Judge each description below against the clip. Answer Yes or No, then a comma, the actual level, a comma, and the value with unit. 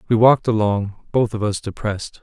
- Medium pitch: No, low, 110 Hz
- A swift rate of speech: No, average, 190 wpm